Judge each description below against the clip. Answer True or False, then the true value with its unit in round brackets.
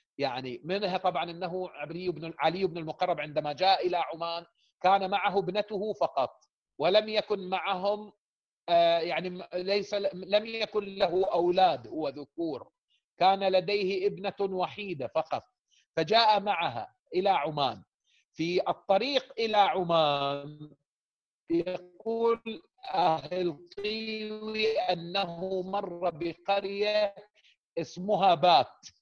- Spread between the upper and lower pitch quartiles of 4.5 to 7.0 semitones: False (3.1 semitones)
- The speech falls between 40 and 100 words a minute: True (95 wpm)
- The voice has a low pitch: False (190 Hz)